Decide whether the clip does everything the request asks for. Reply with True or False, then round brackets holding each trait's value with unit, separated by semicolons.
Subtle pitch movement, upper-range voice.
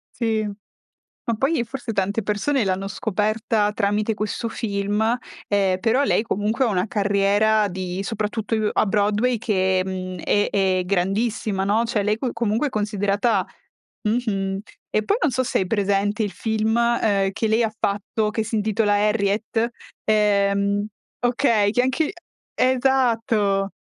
True (2.2 semitones; 210 Hz)